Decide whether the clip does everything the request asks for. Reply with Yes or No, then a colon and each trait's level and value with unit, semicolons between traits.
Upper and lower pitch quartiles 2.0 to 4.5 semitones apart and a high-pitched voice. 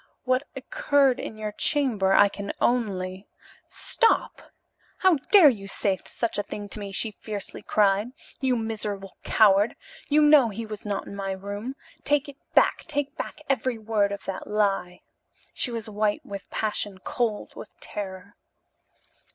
Yes: average, 4.0 semitones; high, 215 Hz